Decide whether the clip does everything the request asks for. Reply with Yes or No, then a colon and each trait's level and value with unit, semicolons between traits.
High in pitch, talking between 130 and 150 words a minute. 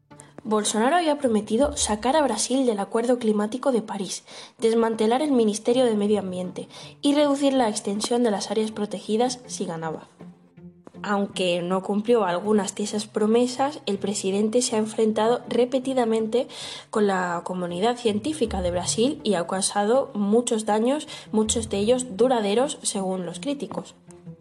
Yes: high, 220 Hz; average, 145 wpm